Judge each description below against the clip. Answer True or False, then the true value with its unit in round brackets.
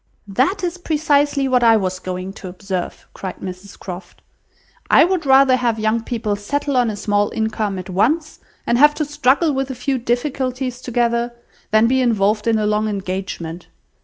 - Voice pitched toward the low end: False (235 Hz)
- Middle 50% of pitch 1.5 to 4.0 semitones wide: False (4.8 semitones)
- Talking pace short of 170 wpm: False (175 wpm)